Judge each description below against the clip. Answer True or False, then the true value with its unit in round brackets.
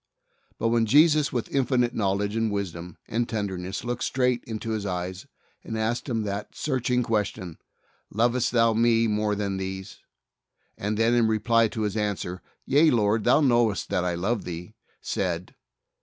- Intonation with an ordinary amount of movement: True (3.3 semitones)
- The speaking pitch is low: True (110 Hz)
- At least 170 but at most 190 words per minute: False (160 wpm)